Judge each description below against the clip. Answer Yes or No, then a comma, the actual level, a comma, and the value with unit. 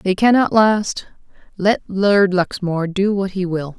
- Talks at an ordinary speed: Yes, average, 145 wpm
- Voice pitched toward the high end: Yes, high, 195 Hz